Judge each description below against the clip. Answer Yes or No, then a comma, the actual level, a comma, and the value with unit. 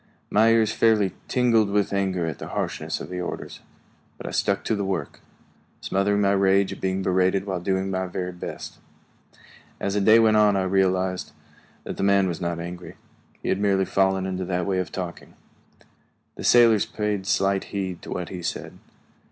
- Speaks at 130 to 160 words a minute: No, average, 185 wpm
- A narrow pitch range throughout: Yes, narrow, 1.7 semitones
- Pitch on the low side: Yes, very low, 95 Hz